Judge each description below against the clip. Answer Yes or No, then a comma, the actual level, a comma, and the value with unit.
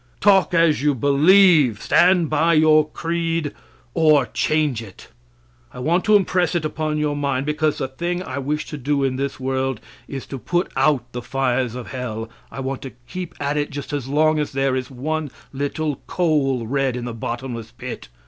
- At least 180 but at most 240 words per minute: Yes, average, 185 wpm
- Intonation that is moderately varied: Yes, average, 3.2 semitones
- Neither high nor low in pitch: Yes, medium, 145 Hz